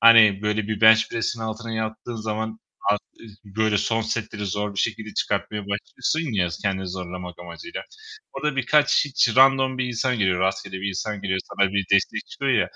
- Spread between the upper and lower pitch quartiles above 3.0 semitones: No, average, 2.7 semitones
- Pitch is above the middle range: No, low, 110 Hz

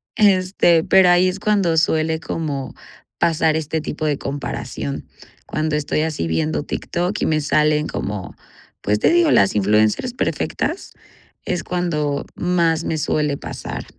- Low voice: No, medium, 155 Hz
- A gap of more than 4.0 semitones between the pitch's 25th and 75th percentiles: No, average, 3.7 semitones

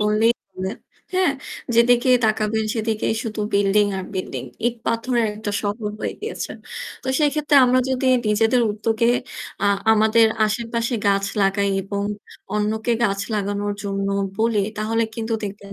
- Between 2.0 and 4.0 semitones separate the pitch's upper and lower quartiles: Yes, narrow, 2.4 semitones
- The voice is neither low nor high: No, high, 220 Hz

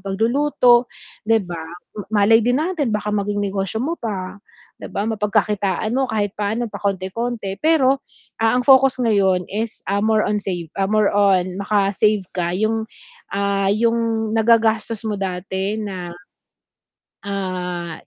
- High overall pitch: Yes, high, 210 Hz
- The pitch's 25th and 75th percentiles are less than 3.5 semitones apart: Yes, narrow, 2.6 semitones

